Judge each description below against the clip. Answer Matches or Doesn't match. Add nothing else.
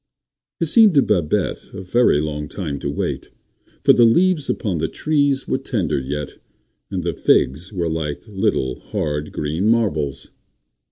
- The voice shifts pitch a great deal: Matches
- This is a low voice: Matches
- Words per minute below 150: Doesn't match